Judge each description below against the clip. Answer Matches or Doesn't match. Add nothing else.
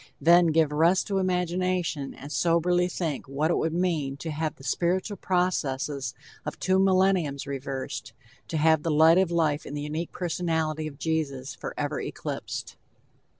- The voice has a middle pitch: Matches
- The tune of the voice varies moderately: Matches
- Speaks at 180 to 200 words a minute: Doesn't match